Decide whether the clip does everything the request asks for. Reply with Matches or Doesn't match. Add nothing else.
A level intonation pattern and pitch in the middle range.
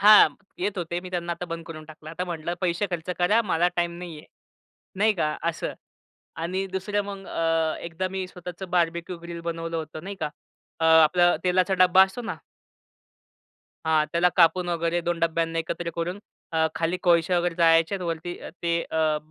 Matches